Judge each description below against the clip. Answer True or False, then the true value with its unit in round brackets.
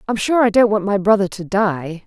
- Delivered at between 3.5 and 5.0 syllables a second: False (5.2 syllables/s)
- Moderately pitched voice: False (200 Hz)